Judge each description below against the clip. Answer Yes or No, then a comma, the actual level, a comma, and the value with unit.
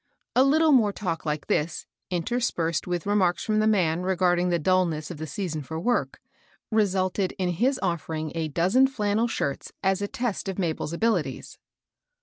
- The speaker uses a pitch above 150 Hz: Yes, medium, 185 Hz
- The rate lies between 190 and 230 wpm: No, average, 170 wpm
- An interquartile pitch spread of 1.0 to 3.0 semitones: No, average, 4.5 semitones